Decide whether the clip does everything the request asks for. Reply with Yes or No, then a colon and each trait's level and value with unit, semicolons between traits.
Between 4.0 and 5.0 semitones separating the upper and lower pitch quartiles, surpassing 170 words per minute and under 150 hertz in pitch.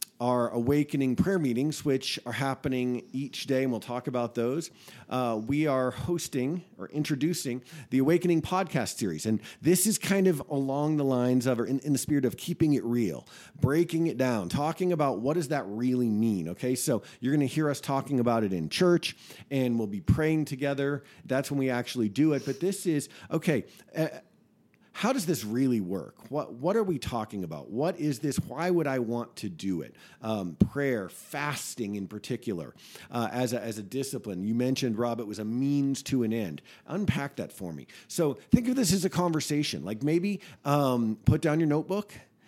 Yes: average, 4.5 semitones; average, 195 wpm; low, 135 Hz